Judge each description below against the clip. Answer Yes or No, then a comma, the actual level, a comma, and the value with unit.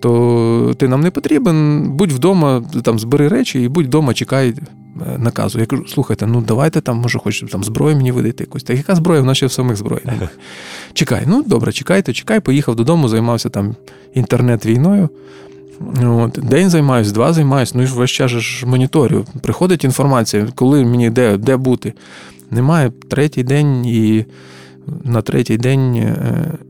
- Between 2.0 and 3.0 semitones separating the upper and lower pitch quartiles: No, average, 3.8 semitones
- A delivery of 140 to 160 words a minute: Yes, fast, 155 wpm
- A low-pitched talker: Yes, low, 125 Hz